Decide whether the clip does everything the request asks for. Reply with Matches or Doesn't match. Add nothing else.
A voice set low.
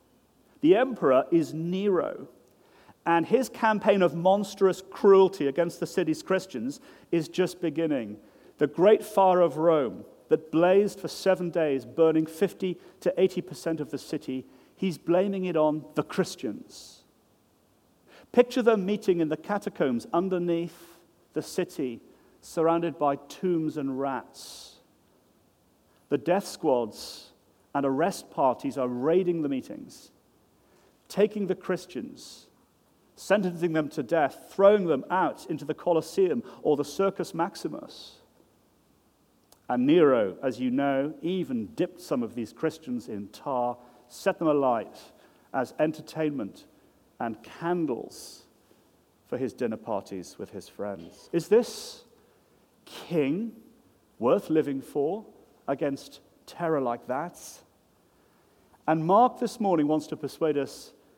Doesn't match